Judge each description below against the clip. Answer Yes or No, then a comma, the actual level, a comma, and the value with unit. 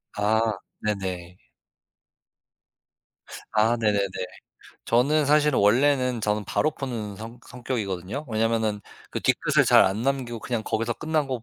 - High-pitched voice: No, low, 115 Hz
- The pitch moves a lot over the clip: No, average, 3.6 semitones